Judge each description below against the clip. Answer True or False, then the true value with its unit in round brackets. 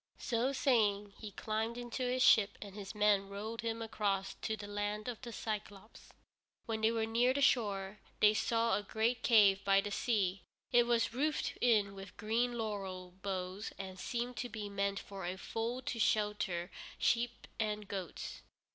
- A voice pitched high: True (215 Hz)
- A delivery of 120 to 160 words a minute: False (175 wpm)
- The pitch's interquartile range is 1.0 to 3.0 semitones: True (2.7 semitones)